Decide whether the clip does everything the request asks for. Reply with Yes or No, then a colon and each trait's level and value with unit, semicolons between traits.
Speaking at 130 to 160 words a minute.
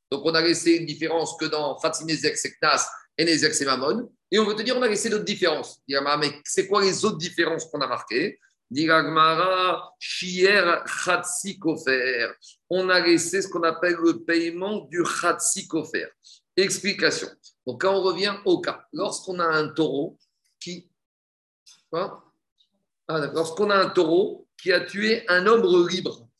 Yes: average, 150 wpm